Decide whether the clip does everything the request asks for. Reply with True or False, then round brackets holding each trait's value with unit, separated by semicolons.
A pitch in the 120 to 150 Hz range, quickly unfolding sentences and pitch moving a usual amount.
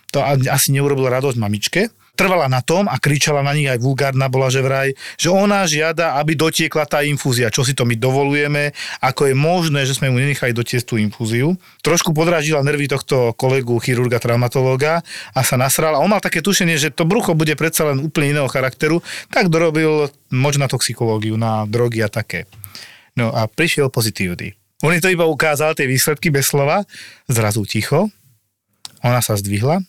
True (140 Hz; 175 wpm; 4.3 semitones)